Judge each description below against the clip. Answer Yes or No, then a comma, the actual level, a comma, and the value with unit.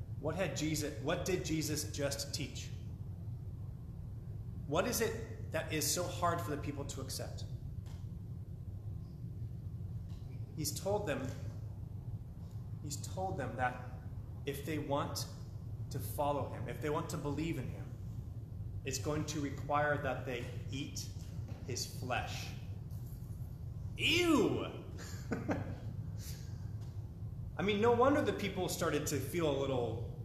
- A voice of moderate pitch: No, low, 120 Hz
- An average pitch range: Yes, average, 4.5 semitones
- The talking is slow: Yes, slow, 120 wpm